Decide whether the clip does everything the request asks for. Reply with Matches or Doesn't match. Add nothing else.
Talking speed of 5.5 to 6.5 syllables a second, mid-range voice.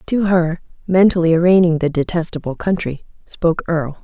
Matches